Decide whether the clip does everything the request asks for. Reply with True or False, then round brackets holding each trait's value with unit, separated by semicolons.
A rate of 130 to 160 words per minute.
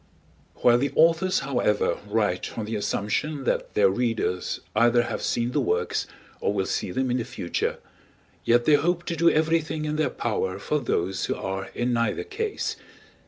False (175 wpm)